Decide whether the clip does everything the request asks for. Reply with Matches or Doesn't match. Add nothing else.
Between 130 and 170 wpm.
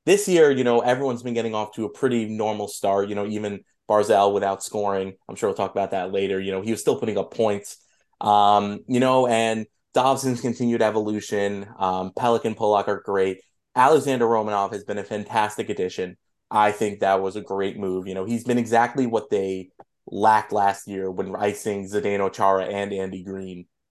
Doesn't match